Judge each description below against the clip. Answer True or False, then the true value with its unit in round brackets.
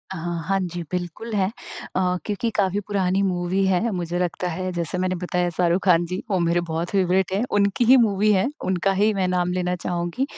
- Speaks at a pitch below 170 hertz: False (185 Hz)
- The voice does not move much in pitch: True (1.9 semitones)